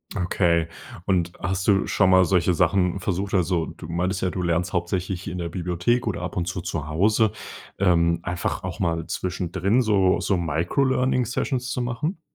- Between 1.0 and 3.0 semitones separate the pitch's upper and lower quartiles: Yes, narrow, 2.6 semitones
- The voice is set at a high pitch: No, very low, 90 Hz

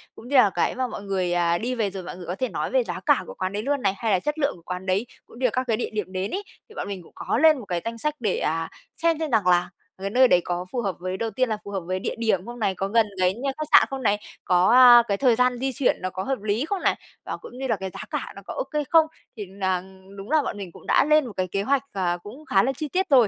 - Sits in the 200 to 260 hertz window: Yes, high, 215 Hz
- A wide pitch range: Yes, wide, 5.7 semitones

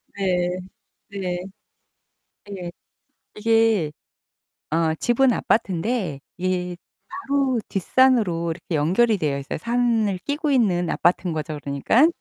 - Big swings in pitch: Yes, wide, 5.8 semitones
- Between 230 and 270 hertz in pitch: No, high, 190 Hz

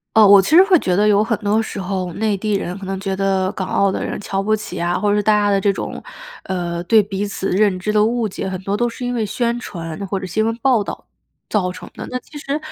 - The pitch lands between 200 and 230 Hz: Yes, high, 205 Hz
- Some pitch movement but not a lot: No, narrow, 2.3 semitones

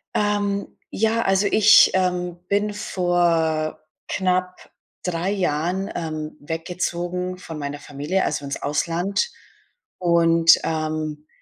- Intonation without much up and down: No, average, 3.4 semitones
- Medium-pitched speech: Yes, medium, 175 Hz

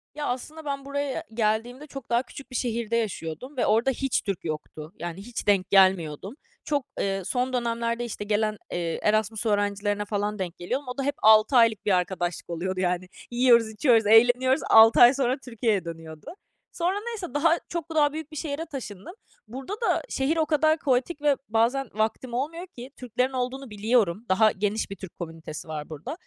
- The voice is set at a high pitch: Yes, high, 230 Hz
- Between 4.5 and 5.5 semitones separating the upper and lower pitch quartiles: Yes, average, 5.1 semitones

